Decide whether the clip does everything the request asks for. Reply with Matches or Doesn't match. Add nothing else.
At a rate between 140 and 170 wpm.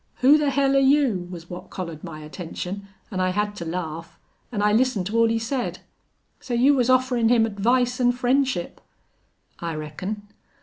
Doesn't match